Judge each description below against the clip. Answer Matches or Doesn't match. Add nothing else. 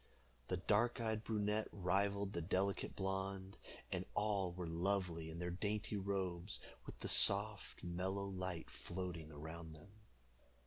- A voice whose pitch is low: Matches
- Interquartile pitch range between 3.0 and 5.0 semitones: Doesn't match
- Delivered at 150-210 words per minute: Doesn't match